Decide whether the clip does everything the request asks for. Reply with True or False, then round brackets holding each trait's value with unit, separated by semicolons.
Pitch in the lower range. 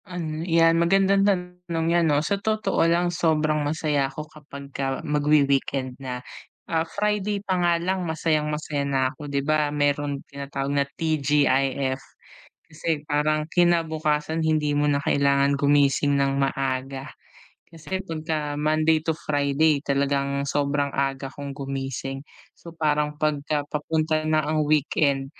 False (150 Hz)